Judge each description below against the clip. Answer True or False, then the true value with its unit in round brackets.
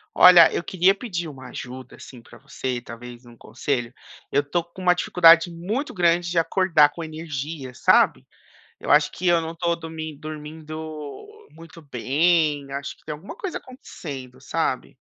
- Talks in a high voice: False (160 Hz)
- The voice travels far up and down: False (3.6 semitones)